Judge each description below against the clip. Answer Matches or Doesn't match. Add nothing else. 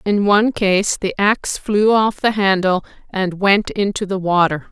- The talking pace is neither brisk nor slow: Matches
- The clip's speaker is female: Matches